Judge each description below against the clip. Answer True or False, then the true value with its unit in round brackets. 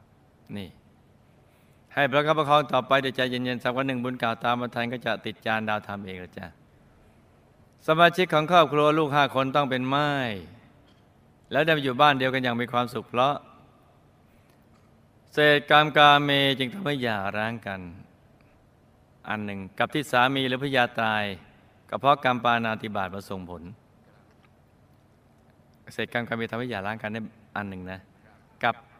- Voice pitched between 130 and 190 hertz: False (120 Hz)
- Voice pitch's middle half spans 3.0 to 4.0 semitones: False (4.4 semitones)